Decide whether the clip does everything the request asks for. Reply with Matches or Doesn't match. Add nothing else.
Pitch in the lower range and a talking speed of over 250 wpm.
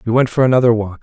Matches